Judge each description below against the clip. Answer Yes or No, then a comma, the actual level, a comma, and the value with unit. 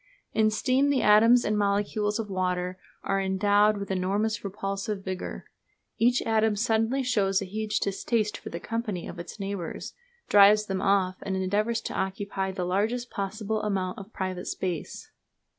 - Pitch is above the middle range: Yes, high, 205 Hz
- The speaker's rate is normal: Yes, average, 160 wpm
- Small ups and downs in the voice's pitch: Yes, narrow, 2.3 semitones